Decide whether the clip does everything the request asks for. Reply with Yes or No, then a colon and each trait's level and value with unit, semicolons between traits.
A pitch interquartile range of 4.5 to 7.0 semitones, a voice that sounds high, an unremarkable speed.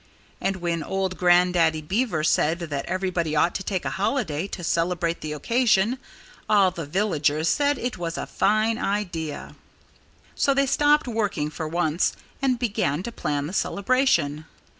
No: average, 5.2 semitones; medium, 180 Hz; average, 155 wpm